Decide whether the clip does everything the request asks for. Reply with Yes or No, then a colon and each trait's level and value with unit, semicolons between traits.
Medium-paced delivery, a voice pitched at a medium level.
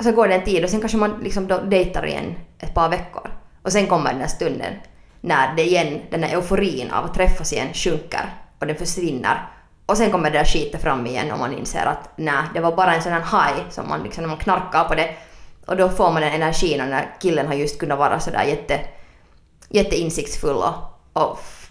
No: fast, 225 wpm; medium, 175 Hz